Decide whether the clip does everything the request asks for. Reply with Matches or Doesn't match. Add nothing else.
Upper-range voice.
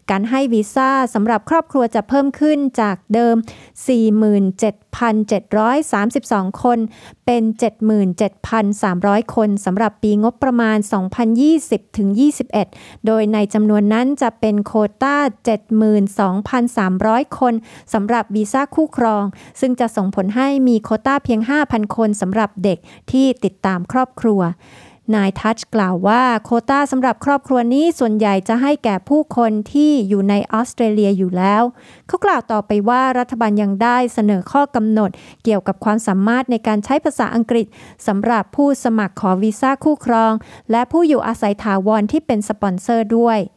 Matches